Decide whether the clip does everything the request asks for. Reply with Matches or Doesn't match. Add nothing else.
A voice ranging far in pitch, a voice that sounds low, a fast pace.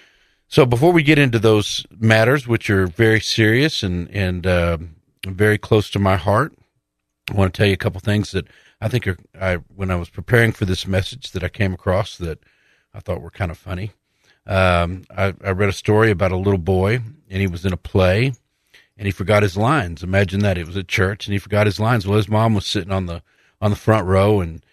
Doesn't match